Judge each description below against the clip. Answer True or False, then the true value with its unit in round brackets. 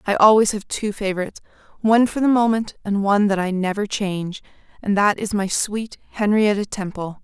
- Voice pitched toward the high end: True (205 Hz)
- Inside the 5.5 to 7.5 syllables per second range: True (5.6 syllables/s)